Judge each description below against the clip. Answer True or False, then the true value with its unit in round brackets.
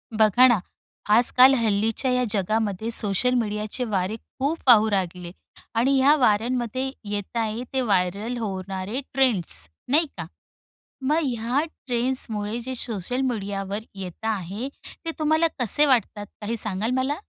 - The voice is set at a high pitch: True (225 Hz)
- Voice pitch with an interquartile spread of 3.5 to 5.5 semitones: True (4.0 semitones)